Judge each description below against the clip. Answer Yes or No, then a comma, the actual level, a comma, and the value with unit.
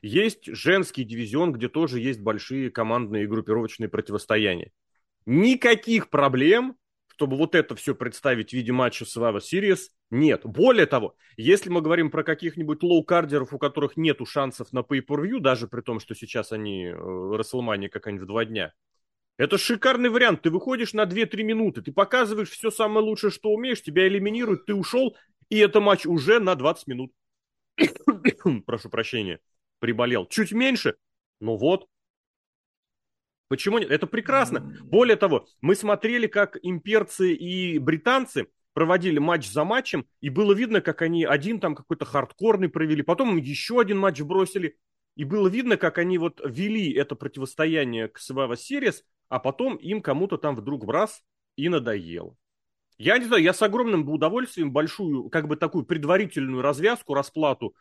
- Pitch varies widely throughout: Yes, wide, 8.0 semitones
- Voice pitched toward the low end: No, medium, 165 Hz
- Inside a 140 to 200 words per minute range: Yes, fast, 160 wpm